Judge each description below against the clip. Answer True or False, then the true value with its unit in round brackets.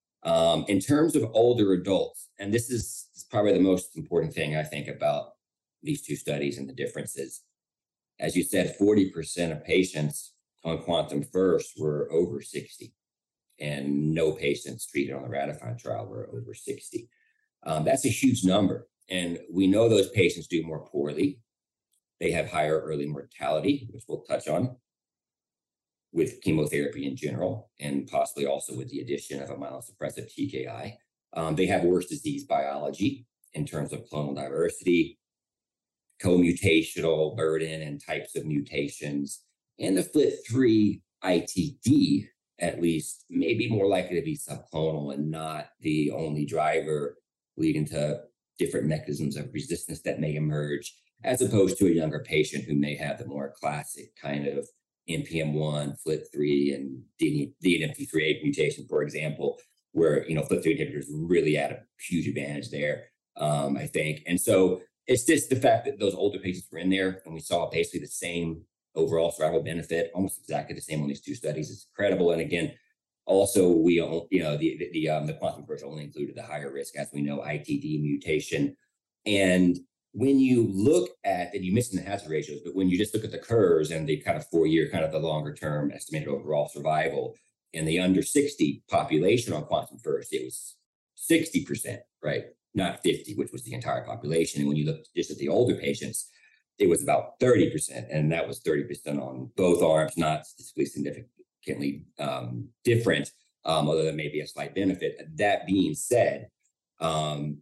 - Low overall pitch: True (80 Hz)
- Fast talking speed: False (170 wpm)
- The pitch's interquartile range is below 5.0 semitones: False (5.3 semitones)